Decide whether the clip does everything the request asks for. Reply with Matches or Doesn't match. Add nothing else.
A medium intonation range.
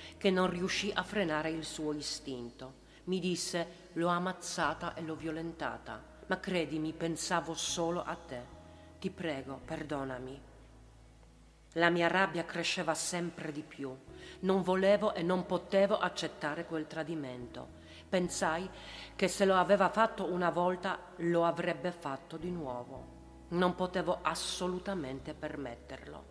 Matches